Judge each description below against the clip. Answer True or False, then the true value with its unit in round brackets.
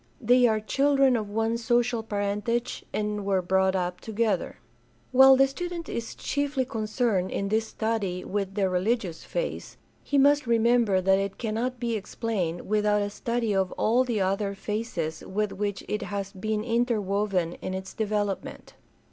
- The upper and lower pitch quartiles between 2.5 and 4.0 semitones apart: True (3.2 semitones)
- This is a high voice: True (215 Hz)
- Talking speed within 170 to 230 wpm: False (155 wpm)